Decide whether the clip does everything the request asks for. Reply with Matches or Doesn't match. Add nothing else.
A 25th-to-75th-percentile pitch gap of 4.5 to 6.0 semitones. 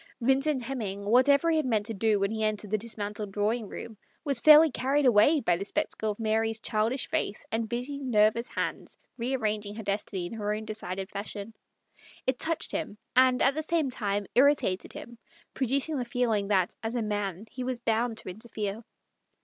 Doesn't match